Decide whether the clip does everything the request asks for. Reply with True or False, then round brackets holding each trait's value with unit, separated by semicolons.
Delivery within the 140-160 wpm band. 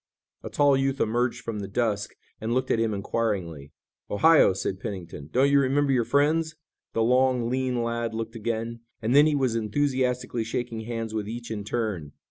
False (180 wpm)